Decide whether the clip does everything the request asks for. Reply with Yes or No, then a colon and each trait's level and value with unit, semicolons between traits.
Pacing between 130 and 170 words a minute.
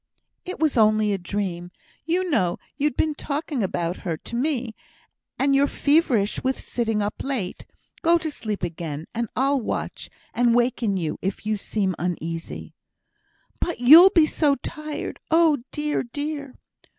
Yes: average, 150 wpm